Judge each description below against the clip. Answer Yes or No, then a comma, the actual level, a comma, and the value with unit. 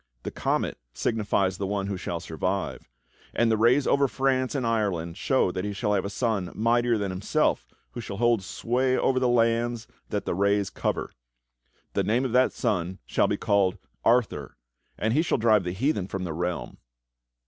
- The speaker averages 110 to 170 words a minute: No, average, 185 wpm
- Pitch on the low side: Yes, low, 105 Hz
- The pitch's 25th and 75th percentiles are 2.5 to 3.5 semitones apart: No, average, 4.1 semitones